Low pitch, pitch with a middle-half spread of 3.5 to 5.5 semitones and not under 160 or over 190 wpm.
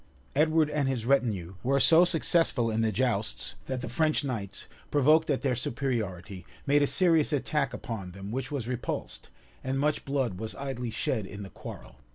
Yes: low, 130 Hz; average, 4.9 semitones; average, 180 wpm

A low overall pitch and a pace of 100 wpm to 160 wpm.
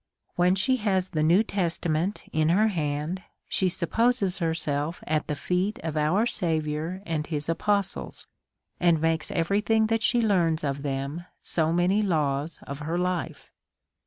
No: medium, 170 Hz; average, 155 wpm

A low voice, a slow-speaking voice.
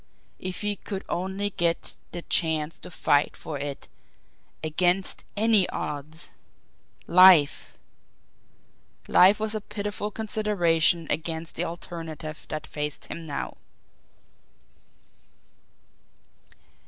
No: medium, 170 Hz; slow, 95 wpm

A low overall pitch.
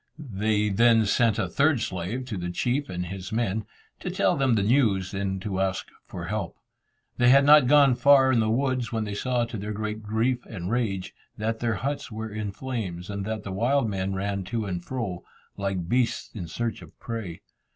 Yes: low, 110 Hz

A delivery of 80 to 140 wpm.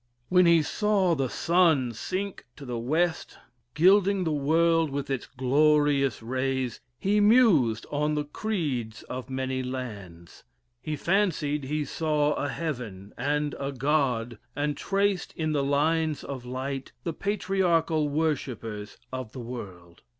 Yes: slow, 135 wpm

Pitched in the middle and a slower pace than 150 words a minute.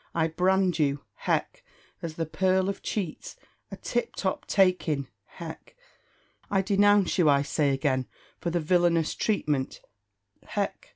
Yes: medium, 175 Hz; average, 140 wpm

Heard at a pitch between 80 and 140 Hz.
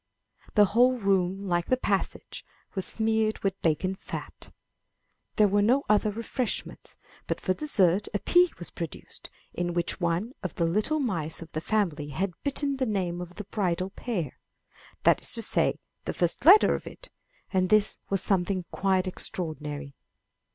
No: high, 195 Hz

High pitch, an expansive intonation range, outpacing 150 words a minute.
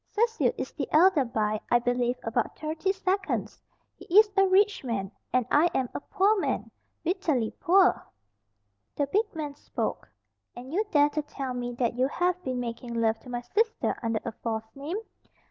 Yes: very high, 285 Hz; wide, 7.7 semitones; average, 180 wpm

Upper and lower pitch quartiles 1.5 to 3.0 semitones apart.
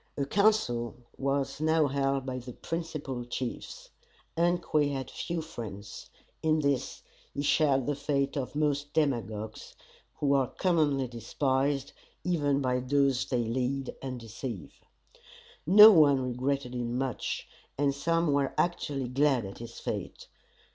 Yes: average, 2.7 semitones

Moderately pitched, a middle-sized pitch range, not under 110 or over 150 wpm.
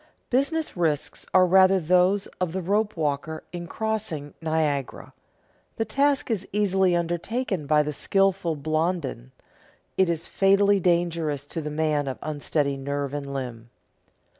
Yes: medium, 170 Hz; average, 4.7 semitones; average, 140 wpm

